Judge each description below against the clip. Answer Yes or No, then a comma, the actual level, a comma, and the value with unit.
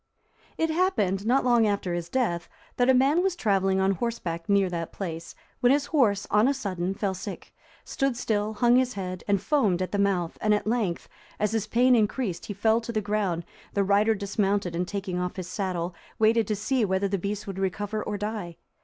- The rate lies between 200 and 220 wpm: Yes, fast, 205 wpm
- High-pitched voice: Yes, high, 205 Hz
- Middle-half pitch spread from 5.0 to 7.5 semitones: No, average, 3.5 semitones